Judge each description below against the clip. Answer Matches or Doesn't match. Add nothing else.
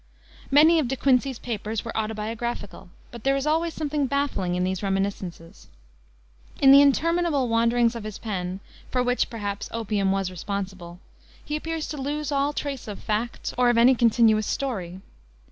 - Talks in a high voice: Matches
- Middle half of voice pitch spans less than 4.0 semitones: Doesn't match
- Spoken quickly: Doesn't match